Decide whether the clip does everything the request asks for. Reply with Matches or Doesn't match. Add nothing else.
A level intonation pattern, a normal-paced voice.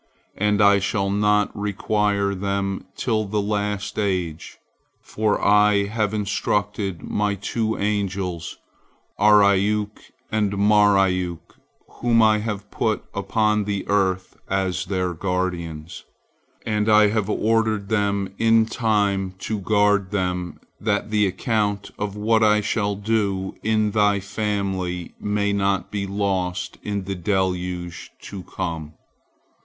Doesn't match